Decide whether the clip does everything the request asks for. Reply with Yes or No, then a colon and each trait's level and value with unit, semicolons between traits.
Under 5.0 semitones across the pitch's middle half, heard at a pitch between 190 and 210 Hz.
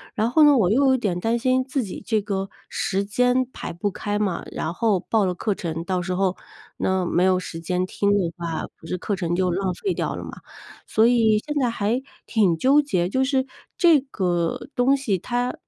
No: average, 5.3 semitones; high, 205 Hz